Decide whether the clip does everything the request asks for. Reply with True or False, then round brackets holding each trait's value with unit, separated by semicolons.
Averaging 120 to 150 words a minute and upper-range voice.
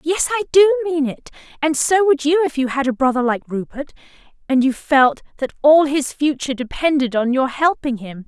False (205 wpm; 285 Hz)